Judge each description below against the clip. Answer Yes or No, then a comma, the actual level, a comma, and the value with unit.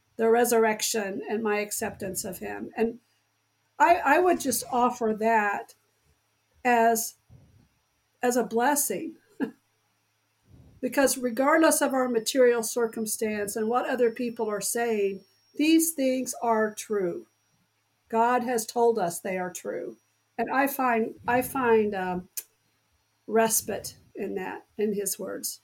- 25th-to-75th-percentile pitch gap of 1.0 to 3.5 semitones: Yes, average, 3.2 semitones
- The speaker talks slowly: Yes, slow, 125 wpm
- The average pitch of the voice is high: Yes, high, 230 Hz